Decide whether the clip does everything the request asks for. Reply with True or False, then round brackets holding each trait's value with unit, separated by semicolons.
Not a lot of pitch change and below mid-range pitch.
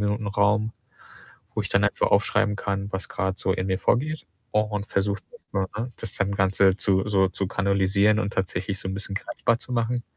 True (1.7 semitones; 100 Hz)